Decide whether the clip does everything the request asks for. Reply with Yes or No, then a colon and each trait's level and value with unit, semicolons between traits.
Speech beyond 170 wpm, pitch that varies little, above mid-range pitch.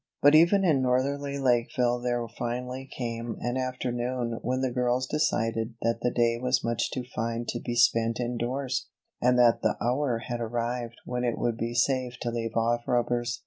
No: average, 180 wpm; narrow, 1.5 semitones; low, 120 Hz